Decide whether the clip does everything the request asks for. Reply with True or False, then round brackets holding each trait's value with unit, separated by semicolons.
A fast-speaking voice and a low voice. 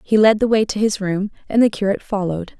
False (255 wpm; 205 Hz)